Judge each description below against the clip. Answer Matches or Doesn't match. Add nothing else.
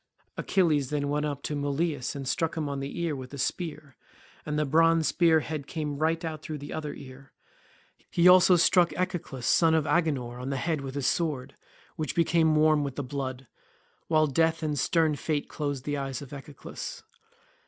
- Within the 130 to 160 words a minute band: Doesn't match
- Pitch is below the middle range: Doesn't match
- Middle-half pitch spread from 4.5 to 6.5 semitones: Doesn't match